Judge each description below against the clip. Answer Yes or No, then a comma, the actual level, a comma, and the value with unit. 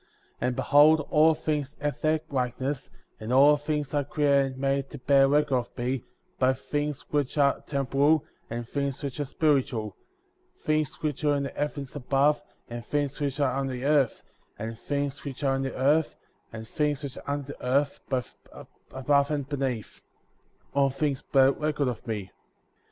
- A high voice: No, medium, 140 Hz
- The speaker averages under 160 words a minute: No, average, 185 wpm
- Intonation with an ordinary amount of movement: No, narrow, 2.0 semitones